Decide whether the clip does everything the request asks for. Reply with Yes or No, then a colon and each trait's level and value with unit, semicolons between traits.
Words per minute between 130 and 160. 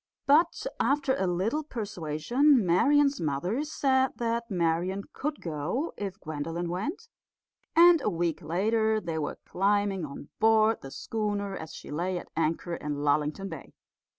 Yes: average, 145 wpm